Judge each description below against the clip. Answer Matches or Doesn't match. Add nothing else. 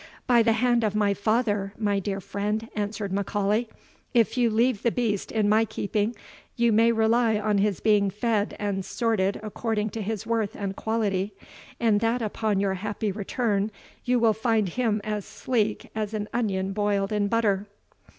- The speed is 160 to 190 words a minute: Matches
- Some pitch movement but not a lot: Doesn't match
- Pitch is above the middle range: Matches